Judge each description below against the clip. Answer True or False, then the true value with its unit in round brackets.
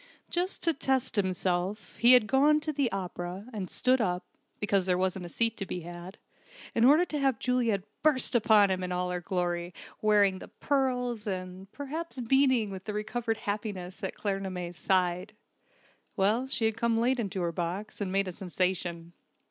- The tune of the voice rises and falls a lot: False (5.0 semitones)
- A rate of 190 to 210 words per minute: False (175 wpm)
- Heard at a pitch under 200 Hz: False (205 Hz)